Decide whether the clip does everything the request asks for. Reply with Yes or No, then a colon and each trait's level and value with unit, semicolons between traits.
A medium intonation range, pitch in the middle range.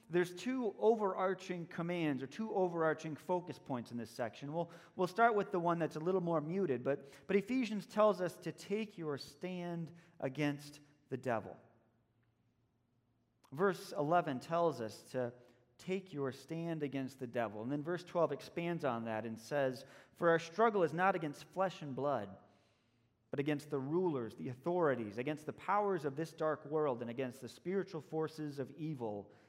No: wide, 5.8 semitones; medium, 150 Hz